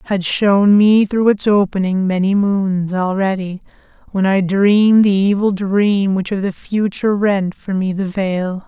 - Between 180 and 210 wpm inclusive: No, average, 165 wpm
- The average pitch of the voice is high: Yes, high, 195 Hz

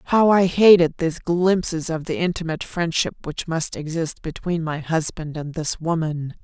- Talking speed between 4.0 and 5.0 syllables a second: Yes, 4.8 syllables/s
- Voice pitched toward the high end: No, medium, 165 Hz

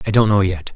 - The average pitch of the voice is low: Yes, low, 100 Hz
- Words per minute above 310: Yes, fast, 320 wpm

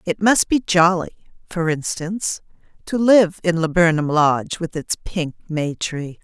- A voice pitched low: No, medium, 170 Hz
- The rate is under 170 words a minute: Yes, average, 155 wpm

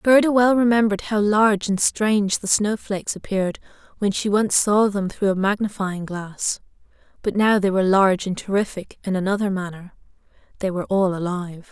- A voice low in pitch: No, high, 200 Hz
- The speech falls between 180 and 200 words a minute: No, average, 170 wpm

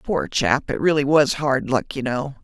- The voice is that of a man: No, female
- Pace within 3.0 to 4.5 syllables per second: Yes, 4.4 syllables/s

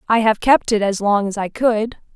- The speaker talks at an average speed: No, fast, 250 wpm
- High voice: Yes, high, 215 Hz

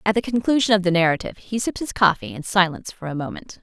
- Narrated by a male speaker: No, female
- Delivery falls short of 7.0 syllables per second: No, 7.1 syllables/s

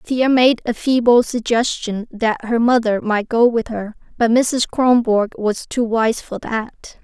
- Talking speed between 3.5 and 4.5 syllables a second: Yes, 3.8 syllables/s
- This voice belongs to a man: No, female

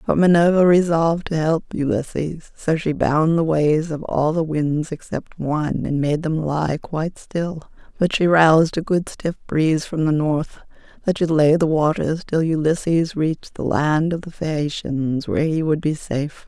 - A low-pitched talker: No, medium, 155 Hz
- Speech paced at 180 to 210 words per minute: Yes, average, 185 wpm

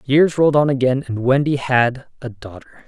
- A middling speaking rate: Yes, average, 190 wpm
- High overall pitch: No, low, 130 Hz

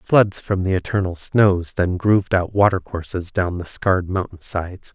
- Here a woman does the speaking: No, male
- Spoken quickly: No, average, 160 wpm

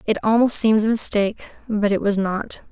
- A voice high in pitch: Yes, high, 210 Hz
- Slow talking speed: No, average, 200 wpm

